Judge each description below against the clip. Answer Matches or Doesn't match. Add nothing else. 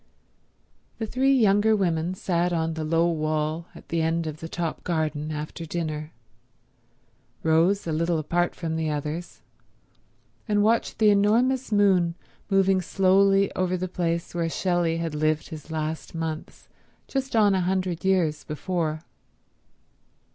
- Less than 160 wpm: Matches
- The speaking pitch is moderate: Matches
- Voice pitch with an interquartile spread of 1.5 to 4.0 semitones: Matches